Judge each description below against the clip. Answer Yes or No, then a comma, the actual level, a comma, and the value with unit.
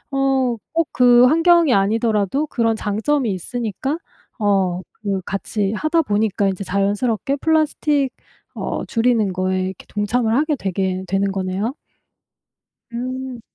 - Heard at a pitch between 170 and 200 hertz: No, high, 225 Hz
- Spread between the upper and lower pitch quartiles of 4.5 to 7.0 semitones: Yes, average, 5.2 semitones